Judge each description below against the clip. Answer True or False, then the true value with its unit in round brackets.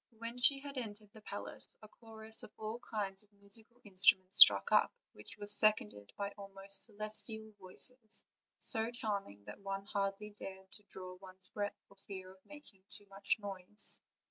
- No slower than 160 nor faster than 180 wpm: True (170 wpm)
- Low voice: False (205 Hz)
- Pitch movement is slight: True (2.2 semitones)